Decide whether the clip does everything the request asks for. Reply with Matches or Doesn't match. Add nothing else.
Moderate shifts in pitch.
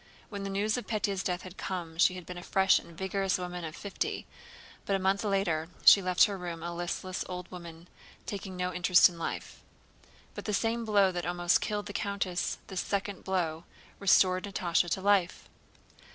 Doesn't match